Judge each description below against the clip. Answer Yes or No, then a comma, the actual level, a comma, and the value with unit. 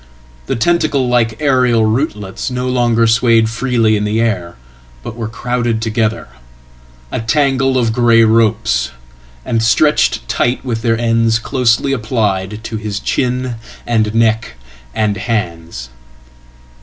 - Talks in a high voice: No, low, 115 Hz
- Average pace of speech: No, slow, 120 wpm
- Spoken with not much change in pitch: Yes, narrow, 2.2 semitones